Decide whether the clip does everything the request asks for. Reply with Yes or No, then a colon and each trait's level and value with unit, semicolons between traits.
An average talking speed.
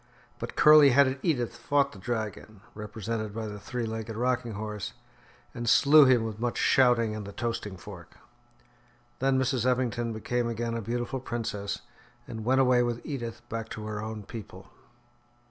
Yes: average, 165 wpm